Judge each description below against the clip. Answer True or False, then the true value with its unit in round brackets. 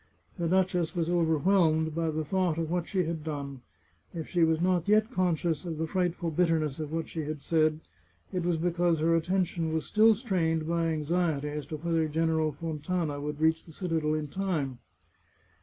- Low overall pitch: False (165 Hz)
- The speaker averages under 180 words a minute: False (185 wpm)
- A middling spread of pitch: False (2.1 semitones)